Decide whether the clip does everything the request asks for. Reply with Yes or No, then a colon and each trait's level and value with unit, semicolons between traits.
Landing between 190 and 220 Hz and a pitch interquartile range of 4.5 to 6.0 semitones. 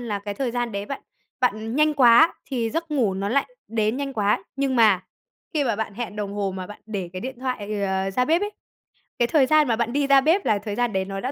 No: high, 230 Hz; average, 5.0 semitones